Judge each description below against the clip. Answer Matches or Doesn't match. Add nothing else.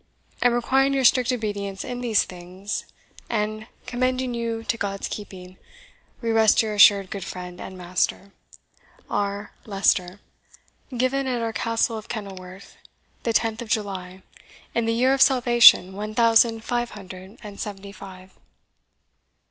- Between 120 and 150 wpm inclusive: Matches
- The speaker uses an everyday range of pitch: Matches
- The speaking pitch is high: Matches